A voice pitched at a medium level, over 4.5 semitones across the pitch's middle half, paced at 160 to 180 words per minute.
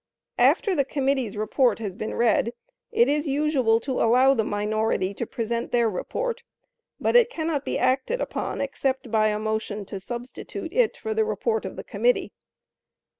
No: very high, 255 Hz; wide, 5.6 semitones; average, 170 wpm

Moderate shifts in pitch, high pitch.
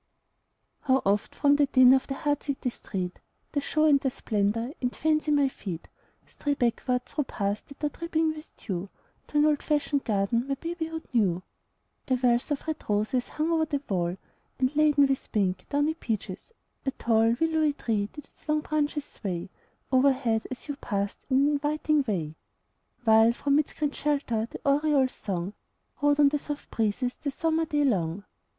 Yes: average, 5.0 semitones; very high, 270 Hz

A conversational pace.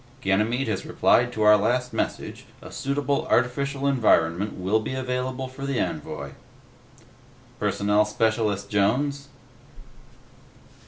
No: slow, 110 wpm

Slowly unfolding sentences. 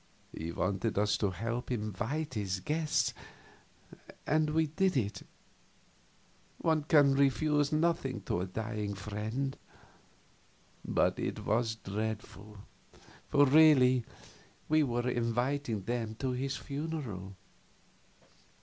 Yes: slow, 110 wpm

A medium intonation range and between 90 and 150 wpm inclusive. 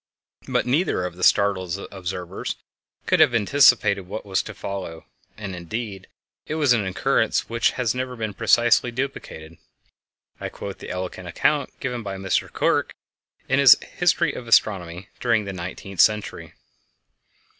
Yes: average, 4.3 semitones; average, 145 wpm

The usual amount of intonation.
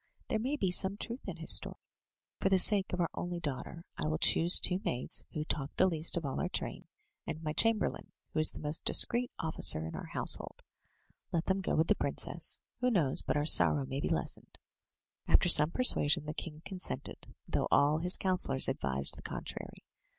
Yes: average, 4.3 semitones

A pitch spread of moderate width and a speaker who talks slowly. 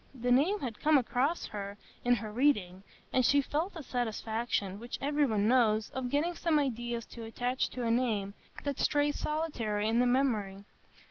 No: average, 4.7 semitones; average, 180 wpm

